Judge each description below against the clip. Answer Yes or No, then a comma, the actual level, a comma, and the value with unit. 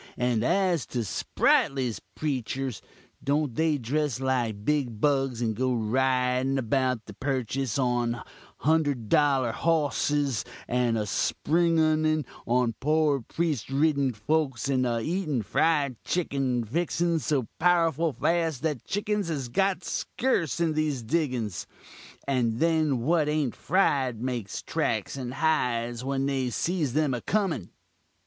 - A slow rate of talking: Yes, slow, 125 wpm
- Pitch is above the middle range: No, low, 135 Hz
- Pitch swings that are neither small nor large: Yes, average, 4.2 semitones